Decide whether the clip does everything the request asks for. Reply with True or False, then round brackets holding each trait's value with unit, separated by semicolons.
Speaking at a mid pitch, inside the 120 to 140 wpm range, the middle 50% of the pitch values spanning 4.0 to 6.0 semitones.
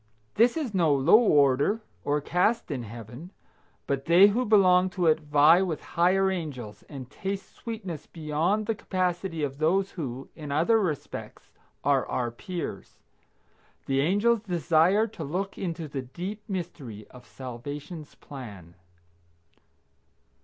True (165 Hz; 135 wpm; 5.5 semitones)